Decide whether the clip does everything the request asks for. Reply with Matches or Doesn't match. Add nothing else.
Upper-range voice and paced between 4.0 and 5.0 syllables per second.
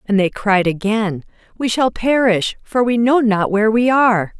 Matches